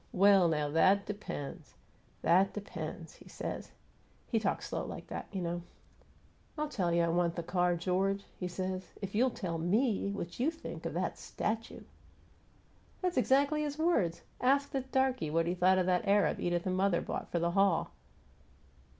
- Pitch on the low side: No, high, 190 Hz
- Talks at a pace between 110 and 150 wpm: No, average, 180 wpm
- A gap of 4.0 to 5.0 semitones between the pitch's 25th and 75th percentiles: Yes, average, 4.7 semitones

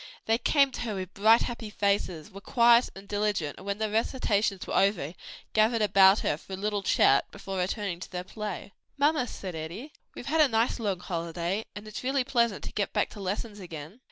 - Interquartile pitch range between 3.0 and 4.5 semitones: Yes, average, 3.5 semitones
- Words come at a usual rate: No, fast, 210 wpm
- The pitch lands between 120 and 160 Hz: No, high, 205 Hz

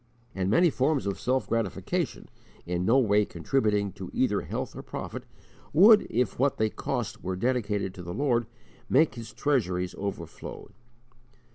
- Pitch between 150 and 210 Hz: No, low, 110 Hz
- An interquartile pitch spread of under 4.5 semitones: No, average, 5.3 semitones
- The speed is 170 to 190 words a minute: No, average, 150 wpm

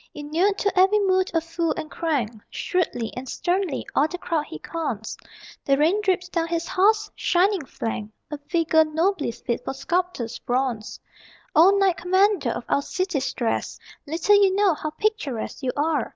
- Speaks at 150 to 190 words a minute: Yes, average, 165 wpm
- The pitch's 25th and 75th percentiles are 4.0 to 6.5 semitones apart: Yes, average, 5.1 semitones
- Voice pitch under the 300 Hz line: No, very high, 330 Hz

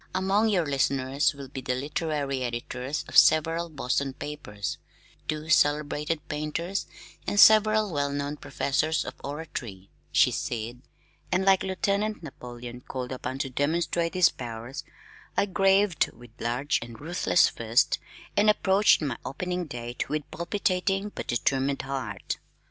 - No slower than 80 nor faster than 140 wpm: Yes, slow, 135 wpm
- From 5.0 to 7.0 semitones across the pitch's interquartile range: Yes, wide, 5.5 semitones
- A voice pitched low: No, medium, 145 Hz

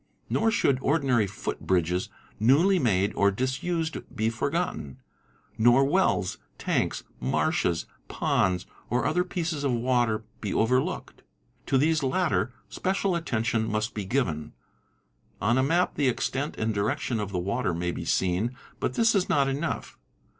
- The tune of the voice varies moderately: No, wide, 7.3 semitones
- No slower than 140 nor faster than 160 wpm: Yes, average, 150 wpm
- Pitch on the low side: Yes, low, 125 Hz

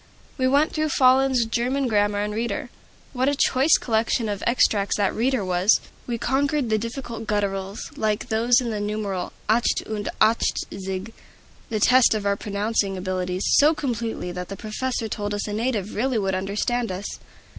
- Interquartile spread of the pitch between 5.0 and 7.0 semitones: No, average, 3.6 semitones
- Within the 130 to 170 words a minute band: Yes, average, 165 wpm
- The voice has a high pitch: Yes, high, 220 Hz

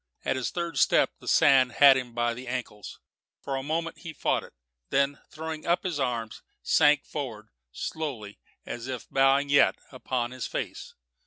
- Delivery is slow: No, average, 175 wpm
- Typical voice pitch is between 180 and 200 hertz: No, low, 135 Hz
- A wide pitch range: No, average, 3.4 semitones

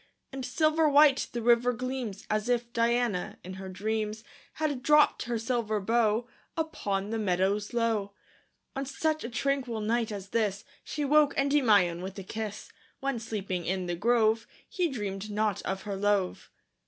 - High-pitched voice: Yes, high, 225 Hz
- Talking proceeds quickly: No, average, 160 wpm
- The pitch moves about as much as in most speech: Yes, average, 4.0 semitones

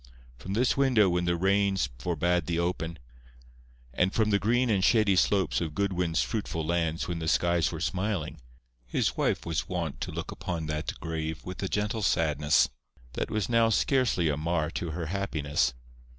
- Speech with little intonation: No, average, 3.7 semitones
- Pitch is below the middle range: Yes, very low, 85 Hz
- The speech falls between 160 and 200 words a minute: Yes, average, 175 wpm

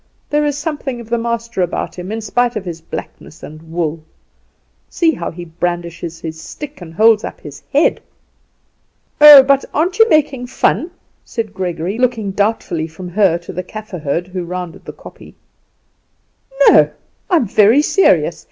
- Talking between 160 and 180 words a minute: Yes, average, 165 wpm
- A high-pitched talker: Yes, high, 205 Hz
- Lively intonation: Yes, wide, 6.7 semitones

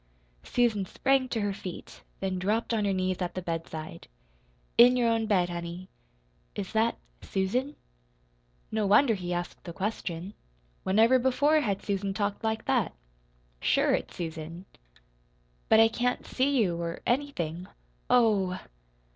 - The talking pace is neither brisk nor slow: Yes, average, 145 wpm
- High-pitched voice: Yes, high, 200 Hz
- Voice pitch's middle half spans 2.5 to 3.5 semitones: No, average, 4.4 semitones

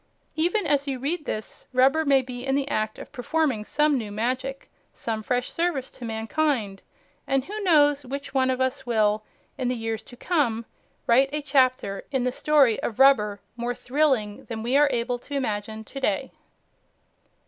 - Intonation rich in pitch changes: No, average, 3.9 semitones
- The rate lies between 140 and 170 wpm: No, average, 180 wpm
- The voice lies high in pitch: Yes, very high, 255 Hz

